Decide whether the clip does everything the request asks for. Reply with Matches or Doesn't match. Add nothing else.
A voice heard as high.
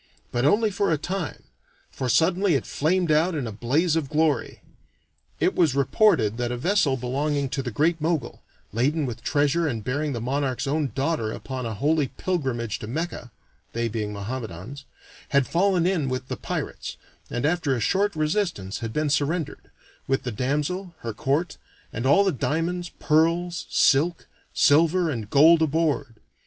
Doesn't match